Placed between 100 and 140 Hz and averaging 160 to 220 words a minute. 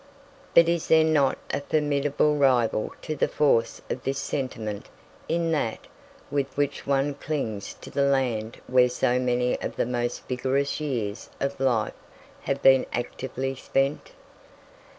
No: low, 135 Hz; average, 145 wpm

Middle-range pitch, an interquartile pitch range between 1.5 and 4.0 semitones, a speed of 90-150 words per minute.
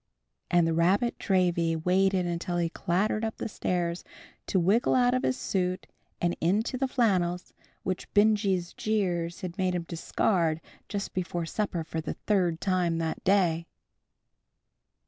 Yes: medium, 180 Hz; average, 3.0 semitones; average, 145 wpm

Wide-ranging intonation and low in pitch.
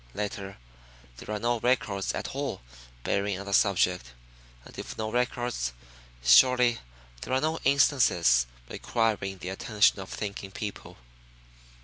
No: average, 4.0 semitones; low, 105 Hz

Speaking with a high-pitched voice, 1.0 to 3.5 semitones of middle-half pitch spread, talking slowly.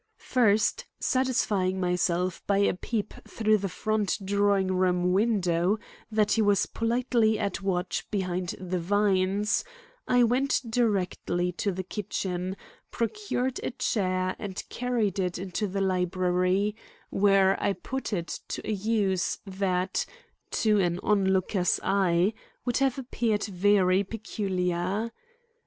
Yes: high, 195 Hz; average, 2.8 semitones; slow, 125 wpm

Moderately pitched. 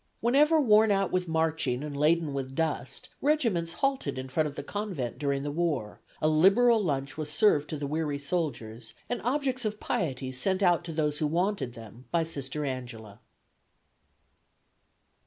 Yes: medium, 155 Hz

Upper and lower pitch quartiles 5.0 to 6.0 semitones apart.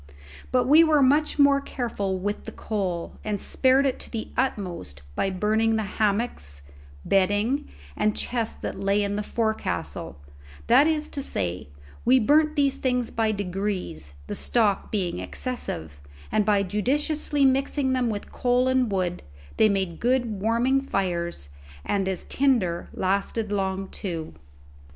Yes: average, 5.3 semitones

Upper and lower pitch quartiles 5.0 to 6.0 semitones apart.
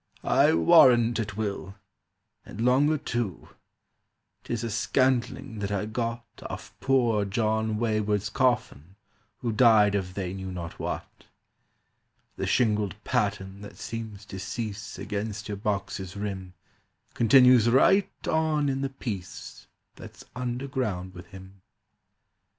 No: average, 3.4 semitones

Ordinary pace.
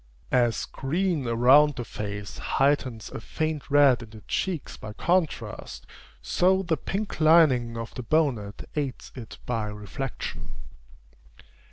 No: slow, 130 wpm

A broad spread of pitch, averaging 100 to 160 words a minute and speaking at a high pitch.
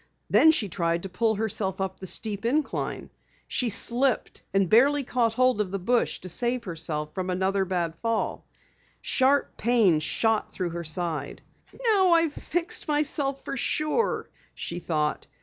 Yes: wide, 6.3 semitones; average, 155 wpm; high, 215 Hz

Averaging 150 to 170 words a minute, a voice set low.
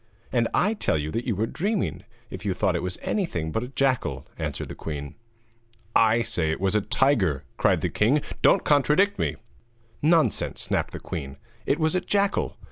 No: average, 190 wpm; low, 115 Hz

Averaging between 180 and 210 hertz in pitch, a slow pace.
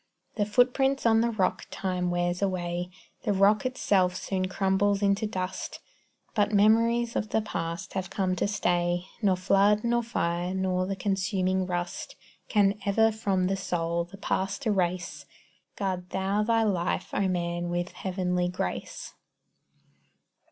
No: high, 190 Hz; average, 145 wpm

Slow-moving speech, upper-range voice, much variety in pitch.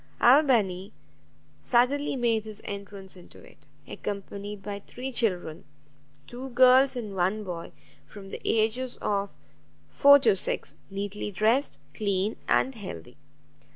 No: slow, 120 wpm; high, 210 Hz; average, 4.2 semitones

